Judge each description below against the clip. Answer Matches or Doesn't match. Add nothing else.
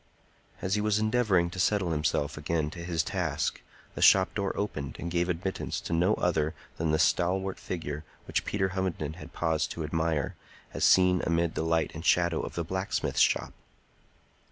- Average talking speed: Matches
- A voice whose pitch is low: Matches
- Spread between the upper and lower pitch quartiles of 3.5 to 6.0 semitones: Doesn't match